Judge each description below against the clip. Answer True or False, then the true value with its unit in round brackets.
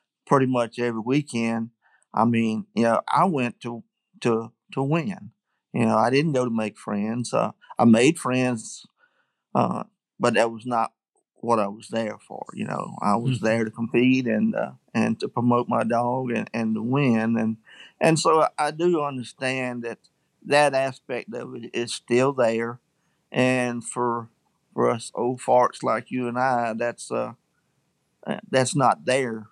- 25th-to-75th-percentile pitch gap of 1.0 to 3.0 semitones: True (2.4 semitones)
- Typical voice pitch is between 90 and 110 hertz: False (120 Hz)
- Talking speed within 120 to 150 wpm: False (170 wpm)